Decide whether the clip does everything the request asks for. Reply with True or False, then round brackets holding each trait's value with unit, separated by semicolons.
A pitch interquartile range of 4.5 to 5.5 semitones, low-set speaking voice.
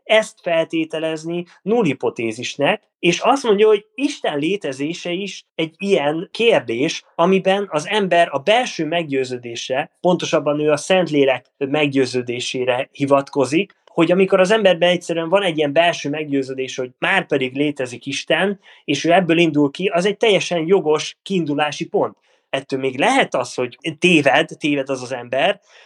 False (5.1 semitones; 165 Hz)